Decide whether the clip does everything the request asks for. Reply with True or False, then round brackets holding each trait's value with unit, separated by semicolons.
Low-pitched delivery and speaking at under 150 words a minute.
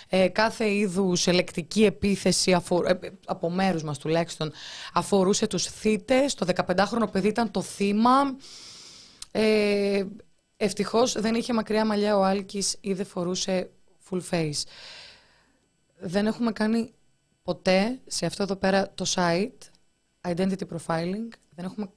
False (195 Hz; 130 wpm)